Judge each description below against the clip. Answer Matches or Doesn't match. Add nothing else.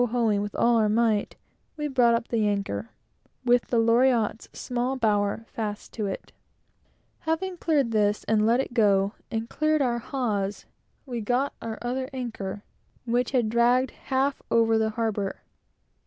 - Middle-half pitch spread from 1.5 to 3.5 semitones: Matches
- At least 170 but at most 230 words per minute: Doesn't match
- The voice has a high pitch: Matches